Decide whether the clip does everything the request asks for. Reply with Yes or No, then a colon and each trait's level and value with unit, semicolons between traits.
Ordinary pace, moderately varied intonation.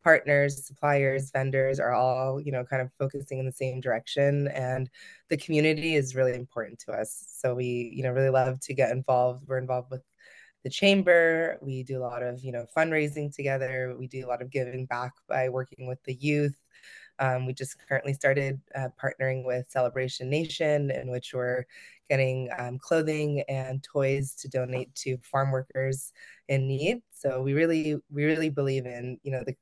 No: average, 185 wpm; narrow, 1.7 semitones